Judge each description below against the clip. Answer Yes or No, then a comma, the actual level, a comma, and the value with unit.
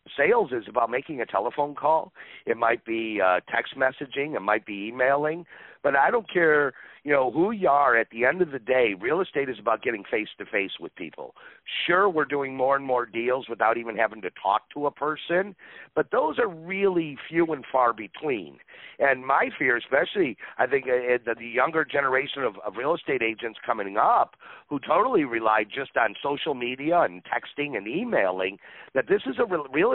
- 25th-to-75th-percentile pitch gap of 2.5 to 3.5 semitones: No, average, 4.8 semitones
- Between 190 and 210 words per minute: Yes, average, 200 wpm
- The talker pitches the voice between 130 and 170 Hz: Yes, low, 135 Hz